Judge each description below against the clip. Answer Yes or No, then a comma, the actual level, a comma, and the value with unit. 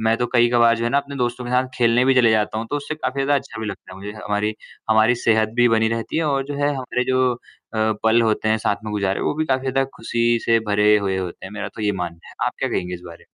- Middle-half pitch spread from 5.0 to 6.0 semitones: No, average, 3.3 semitones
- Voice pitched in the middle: No, low, 115 Hz